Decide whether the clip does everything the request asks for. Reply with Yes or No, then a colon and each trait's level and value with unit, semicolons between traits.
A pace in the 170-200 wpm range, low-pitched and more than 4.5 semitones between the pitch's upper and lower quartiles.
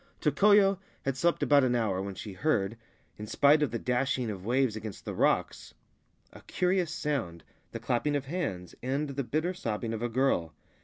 Yes: average, 185 wpm; low, 130 Hz; wide, 5.5 semitones